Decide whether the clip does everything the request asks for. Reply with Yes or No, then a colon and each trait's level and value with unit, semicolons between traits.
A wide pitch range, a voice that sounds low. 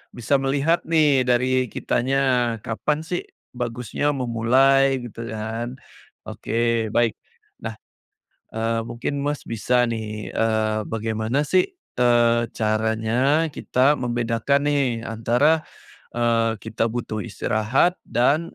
No: average, 3.2 semitones; low, 120 Hz